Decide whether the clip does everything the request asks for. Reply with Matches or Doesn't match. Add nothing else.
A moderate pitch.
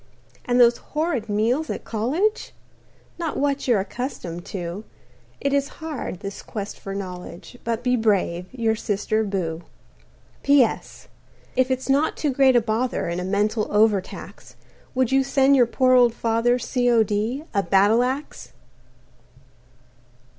Doesn't match